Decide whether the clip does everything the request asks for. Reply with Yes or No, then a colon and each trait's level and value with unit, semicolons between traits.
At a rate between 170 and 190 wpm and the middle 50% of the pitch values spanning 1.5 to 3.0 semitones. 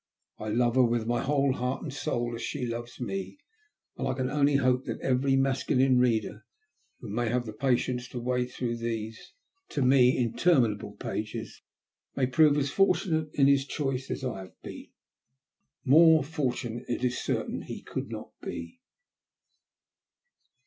No: average, 160 wpm; narrow, 2.5 semitones